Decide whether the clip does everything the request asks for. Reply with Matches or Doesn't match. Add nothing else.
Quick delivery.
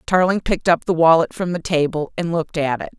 Matches